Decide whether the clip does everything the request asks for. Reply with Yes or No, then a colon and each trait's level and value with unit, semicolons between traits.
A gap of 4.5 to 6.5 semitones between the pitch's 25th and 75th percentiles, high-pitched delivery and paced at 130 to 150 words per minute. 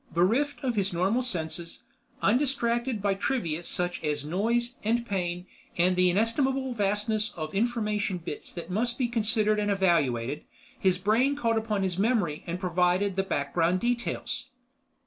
Yes: average, 4.8 semitones; high, 200 Hz; average, 145 wpm